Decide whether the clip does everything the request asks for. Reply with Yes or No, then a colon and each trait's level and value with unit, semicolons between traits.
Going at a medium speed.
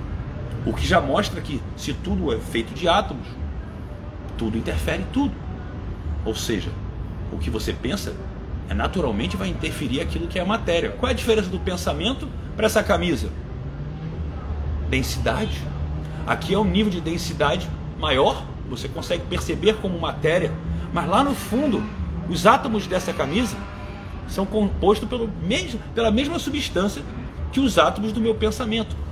Yes: average, 145 wpm